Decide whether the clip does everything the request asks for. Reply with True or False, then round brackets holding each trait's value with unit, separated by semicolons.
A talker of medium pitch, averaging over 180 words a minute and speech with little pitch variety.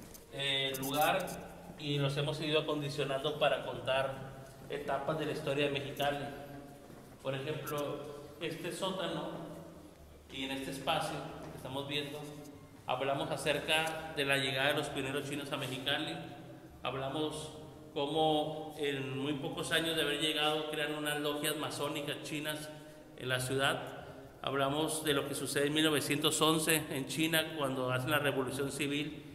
False (145 Hz; 140 wpm; 1.8 semitones)